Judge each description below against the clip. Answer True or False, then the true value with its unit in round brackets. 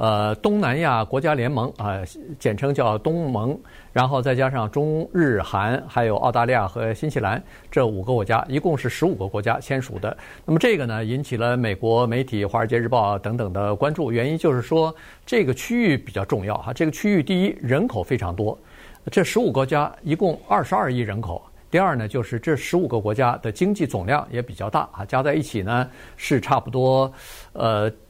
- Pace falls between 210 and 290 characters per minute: False (300 characters per minute)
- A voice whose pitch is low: True (125 Hz)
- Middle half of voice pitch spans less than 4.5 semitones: False (4.9 semitones)